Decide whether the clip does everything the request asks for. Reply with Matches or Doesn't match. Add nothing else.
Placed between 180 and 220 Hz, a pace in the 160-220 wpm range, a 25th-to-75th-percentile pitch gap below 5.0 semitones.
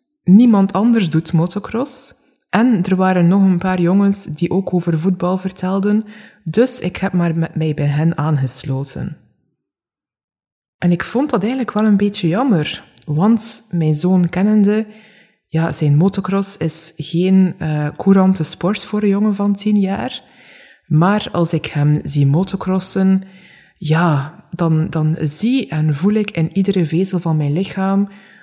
Doesn't match